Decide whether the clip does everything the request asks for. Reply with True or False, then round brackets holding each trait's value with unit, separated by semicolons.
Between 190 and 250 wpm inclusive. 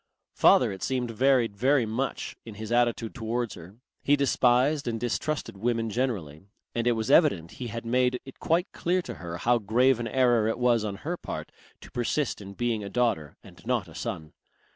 True (195 wpm)